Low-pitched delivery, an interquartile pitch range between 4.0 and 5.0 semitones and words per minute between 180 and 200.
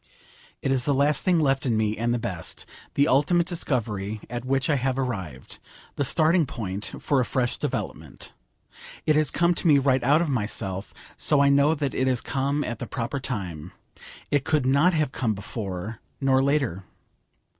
Yes: low, 130 Hz; average, 4.4 semitones; average, 185 wpm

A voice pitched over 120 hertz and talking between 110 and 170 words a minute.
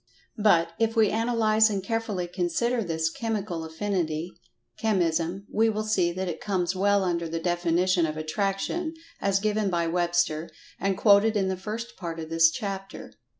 Yes: high, 190 Hz; average, 160 wpm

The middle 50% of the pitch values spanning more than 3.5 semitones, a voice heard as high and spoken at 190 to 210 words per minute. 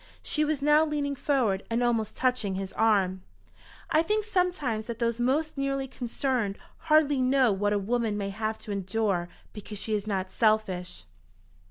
No: average, 5.1 semitones; high, 230 Hz; average, 165 wpm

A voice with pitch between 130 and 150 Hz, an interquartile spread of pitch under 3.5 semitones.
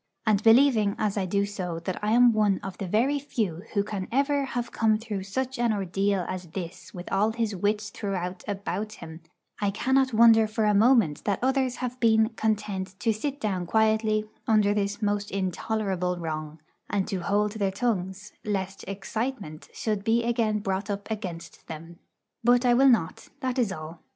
No: high, 210 Hz; average, 3.0 semitones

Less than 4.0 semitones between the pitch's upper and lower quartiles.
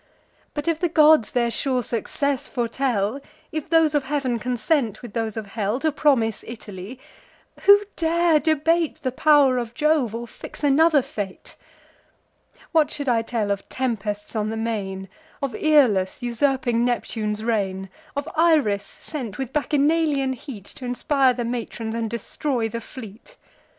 No: average, 4.9 semitones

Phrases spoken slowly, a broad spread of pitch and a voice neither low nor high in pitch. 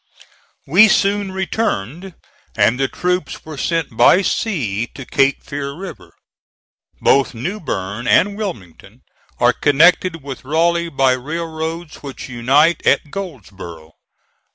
Yes: slow, 120 wpm; wide, 5.8 semitones; medium, 150 Hz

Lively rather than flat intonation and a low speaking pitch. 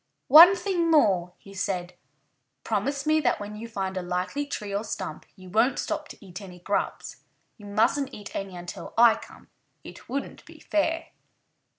No: wide, 6.8 semitones; high, 210 Hz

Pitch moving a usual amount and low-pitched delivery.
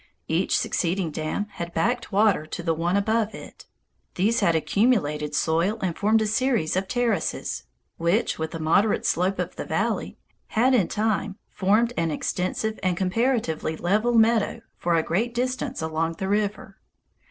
No: average, 5.0 semitones; high, 195 Hz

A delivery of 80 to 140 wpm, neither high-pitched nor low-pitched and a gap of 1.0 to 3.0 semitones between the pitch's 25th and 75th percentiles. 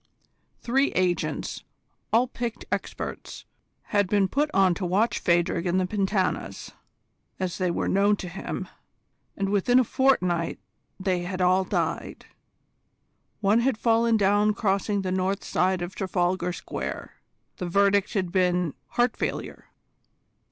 No: slow, 135 wpm; high, 195 Hz; average, 2.7 semitones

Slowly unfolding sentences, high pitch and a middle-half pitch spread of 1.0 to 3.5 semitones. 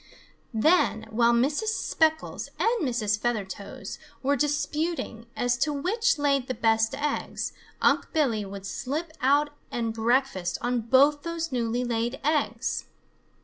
No: slow, 130 wpm; very high, 255 Hz; average, 4.5 semitones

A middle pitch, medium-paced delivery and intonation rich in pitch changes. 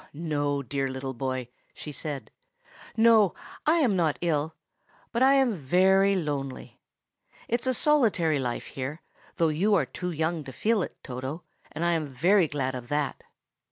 Yes: medium, 160 Hz; average, 160 wpm; wide, 6.0 semitones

